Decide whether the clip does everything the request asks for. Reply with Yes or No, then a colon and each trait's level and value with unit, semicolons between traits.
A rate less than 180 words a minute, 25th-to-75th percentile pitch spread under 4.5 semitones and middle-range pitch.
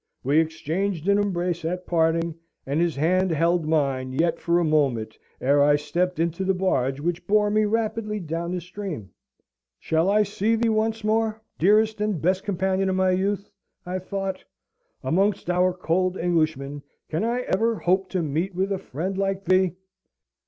Yes: average, 170 wpm; average, 3.5 semitones; medium, 180 Hz